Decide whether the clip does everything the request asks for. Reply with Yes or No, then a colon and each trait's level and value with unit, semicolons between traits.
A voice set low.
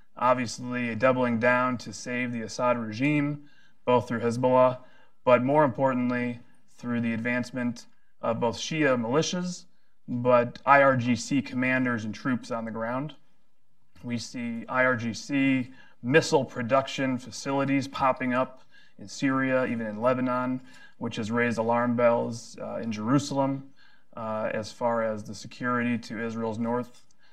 Yes: low, 125 Hz